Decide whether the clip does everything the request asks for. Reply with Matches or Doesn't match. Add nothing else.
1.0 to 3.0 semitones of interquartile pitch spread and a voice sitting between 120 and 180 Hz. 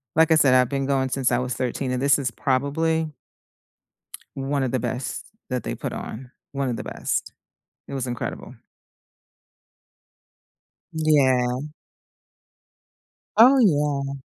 Matches